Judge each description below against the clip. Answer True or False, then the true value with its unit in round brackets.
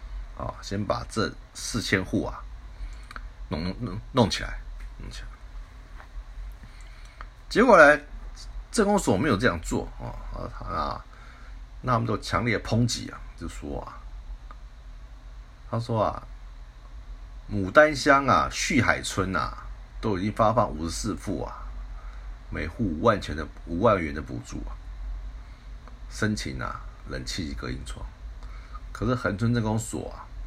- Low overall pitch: True (100 Hz)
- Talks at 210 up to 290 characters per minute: False (185 characters per minute)